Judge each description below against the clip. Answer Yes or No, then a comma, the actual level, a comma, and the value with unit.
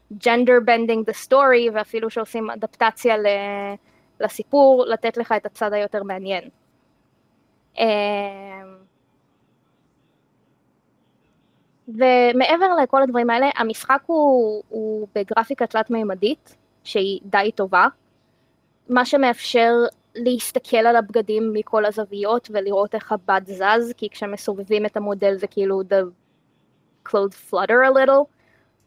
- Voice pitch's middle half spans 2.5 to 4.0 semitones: Yes, average, 2.8 semitones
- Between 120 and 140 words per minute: No, slow, 100 wpm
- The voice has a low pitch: No, high, 220 Hz